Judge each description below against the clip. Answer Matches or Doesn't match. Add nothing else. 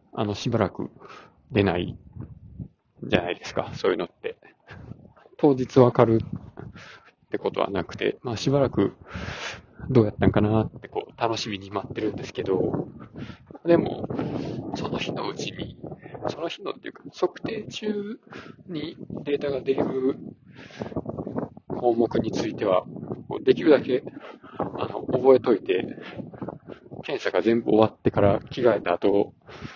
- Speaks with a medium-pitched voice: Doesn't match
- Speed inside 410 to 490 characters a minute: Doesn't match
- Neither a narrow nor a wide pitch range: Matches